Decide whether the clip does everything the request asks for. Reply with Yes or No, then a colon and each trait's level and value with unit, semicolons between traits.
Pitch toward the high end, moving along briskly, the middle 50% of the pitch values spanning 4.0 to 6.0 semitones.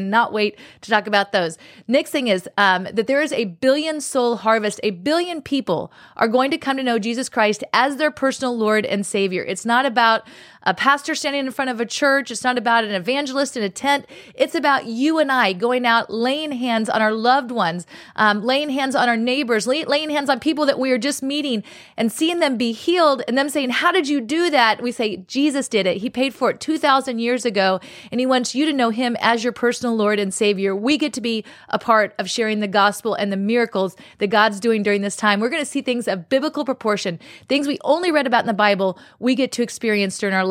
Yes: high, 240 Hz; fast, 240 wpm; average, 4.4 semitones